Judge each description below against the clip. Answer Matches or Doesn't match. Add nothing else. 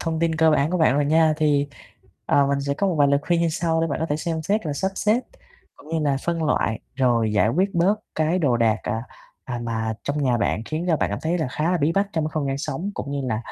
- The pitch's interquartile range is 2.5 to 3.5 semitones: Matches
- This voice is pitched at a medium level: Matches